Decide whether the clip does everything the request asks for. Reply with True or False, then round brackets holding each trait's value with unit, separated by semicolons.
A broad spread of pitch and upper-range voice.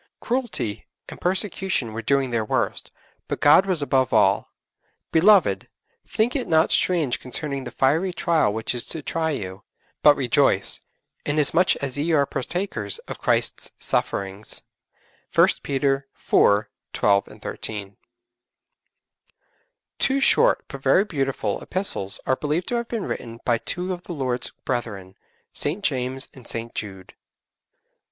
False (7.3 semitones; 140 Hz)